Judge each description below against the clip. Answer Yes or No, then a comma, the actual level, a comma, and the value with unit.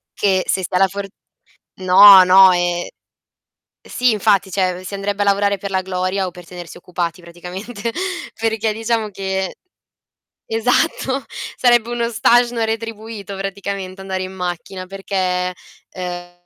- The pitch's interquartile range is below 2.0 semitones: No, average, 2.9 semitones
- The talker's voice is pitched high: Yes, high, 195 Hz